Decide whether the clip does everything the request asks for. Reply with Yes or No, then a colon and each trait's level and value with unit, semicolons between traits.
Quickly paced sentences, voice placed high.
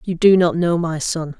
No: fast, 255 wpm; medium, 170 Hz